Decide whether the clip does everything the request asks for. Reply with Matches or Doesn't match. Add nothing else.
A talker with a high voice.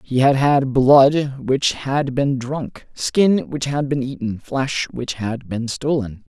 Doesn't match